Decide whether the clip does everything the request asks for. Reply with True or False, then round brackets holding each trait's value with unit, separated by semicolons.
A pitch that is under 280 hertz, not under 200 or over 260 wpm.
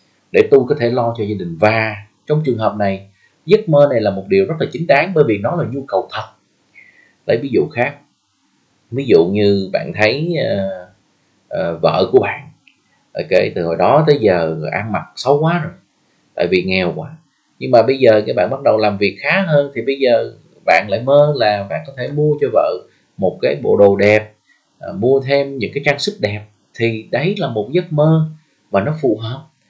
True (140 Hz; 215 wpm)